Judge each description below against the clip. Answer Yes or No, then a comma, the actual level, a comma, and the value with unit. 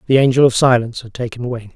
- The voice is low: Yes, low, 120 Hz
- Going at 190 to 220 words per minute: No, fast, 240 wpm